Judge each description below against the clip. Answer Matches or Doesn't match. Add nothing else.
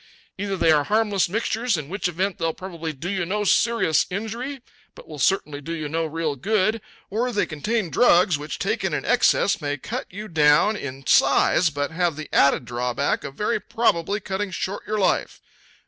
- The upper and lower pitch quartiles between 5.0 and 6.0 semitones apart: Matches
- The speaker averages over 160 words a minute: Matches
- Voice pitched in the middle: Matches